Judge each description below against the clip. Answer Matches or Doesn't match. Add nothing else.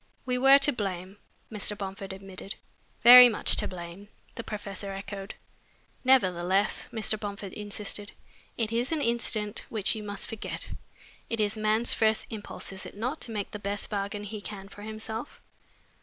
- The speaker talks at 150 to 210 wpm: Matches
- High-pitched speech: Matches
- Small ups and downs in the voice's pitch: Matches